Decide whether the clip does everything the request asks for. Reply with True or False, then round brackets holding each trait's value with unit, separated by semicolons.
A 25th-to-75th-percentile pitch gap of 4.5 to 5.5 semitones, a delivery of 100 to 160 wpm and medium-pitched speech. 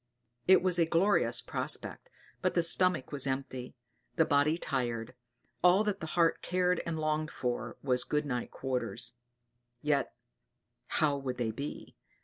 True (5.0 semitones; 145 wpm; 145 Hz)